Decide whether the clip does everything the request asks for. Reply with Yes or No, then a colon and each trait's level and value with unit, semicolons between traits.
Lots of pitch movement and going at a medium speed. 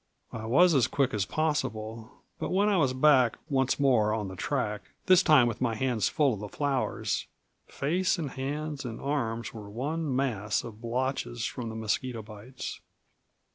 No: average, 4.6 semitones; average, 175 wpm